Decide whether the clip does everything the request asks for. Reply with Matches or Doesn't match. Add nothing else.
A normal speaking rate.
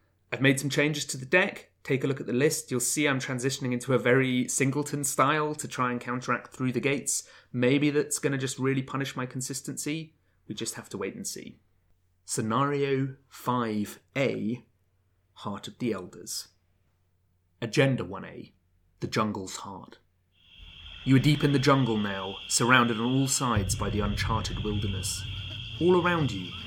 Matches